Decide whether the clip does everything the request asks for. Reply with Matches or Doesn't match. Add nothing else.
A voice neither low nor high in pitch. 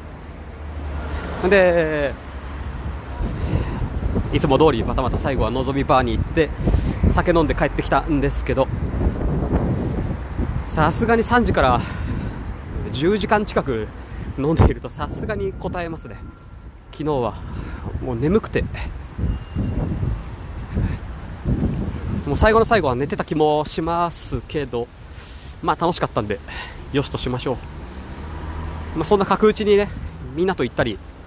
Doesn't match